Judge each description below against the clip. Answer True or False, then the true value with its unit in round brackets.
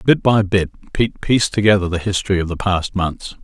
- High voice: False (95 Hz)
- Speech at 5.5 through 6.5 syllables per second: True (5.9 syllables/s)